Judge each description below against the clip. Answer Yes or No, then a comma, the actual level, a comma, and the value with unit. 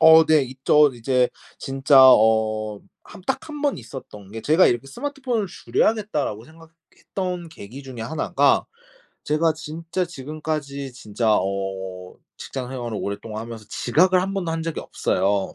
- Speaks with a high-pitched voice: No, medium, 140 Hz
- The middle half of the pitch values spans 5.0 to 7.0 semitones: Yes, wide, 6.7 semitones